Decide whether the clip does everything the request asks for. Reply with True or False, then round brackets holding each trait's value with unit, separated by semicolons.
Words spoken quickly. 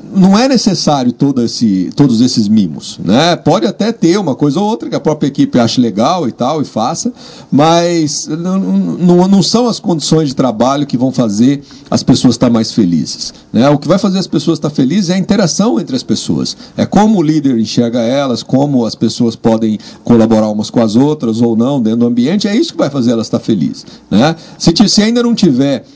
True (215 wpm)